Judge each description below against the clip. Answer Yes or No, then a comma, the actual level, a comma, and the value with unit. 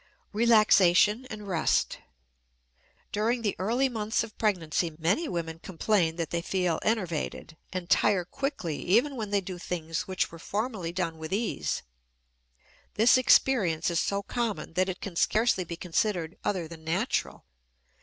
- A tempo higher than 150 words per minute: No, average, 145 wpm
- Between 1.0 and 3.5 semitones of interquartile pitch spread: No, average, 4.4 semitones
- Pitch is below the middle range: No, high, 190 Hz